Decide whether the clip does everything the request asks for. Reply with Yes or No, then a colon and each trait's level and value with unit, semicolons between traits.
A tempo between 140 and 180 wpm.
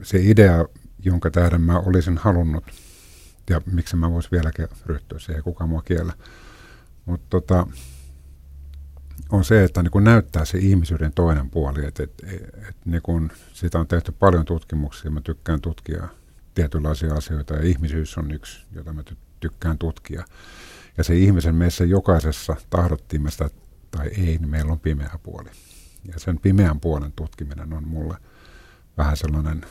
Yes: average, 145 wpm